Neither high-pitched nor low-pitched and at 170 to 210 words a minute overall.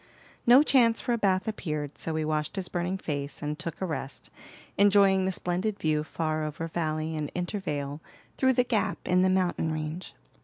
Yes: medium, 175 Hz; average, 185 wpm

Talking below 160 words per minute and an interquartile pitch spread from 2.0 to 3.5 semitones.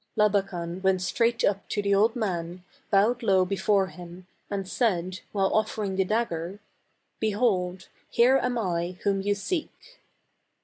Yes: average, 145 wpm; average, 2.9 semitones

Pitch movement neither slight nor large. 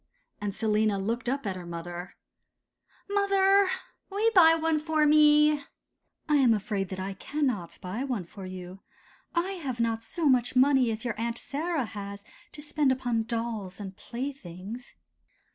No: wide, 7.0 semitones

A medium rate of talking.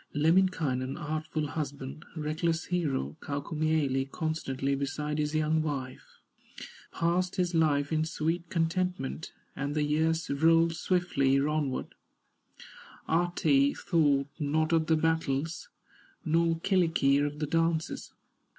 No: slow, 110 wpm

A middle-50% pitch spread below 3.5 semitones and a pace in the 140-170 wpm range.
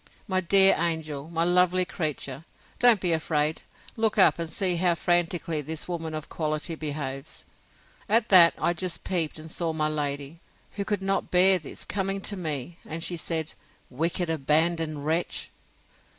Yes: average, 2.8 semitones; average, 160 wpm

